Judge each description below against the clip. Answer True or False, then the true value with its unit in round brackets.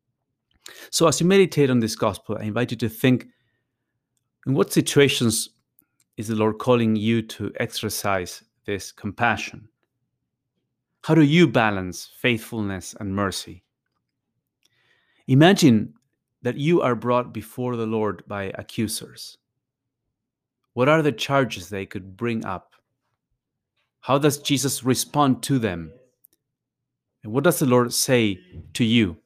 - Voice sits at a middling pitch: False (120 Hz)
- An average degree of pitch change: True (3.4 semitones)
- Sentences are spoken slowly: True (130 wpm)